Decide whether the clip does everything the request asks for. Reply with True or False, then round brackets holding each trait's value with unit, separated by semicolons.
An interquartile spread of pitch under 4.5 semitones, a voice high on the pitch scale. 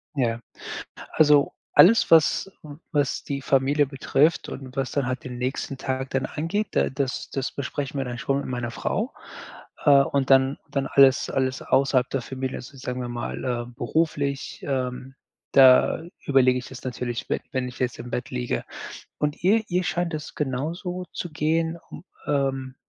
False (2.6 semitones; 135 Hz)